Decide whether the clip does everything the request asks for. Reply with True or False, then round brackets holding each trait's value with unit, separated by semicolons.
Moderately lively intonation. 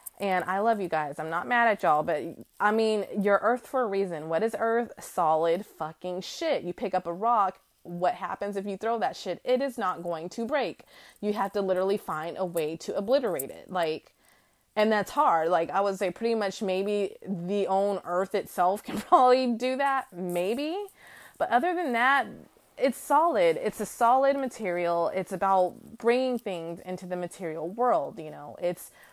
True (5.0 semitones)